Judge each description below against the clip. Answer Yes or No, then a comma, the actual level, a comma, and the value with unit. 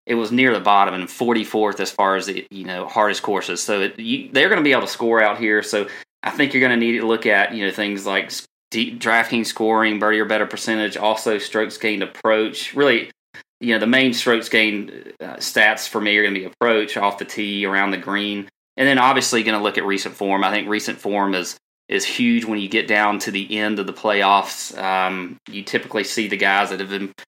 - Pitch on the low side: Yes, low, 105 Hz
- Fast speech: Yes, fast, 240 wpm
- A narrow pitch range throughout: Yes, narrow, 2.3 semitones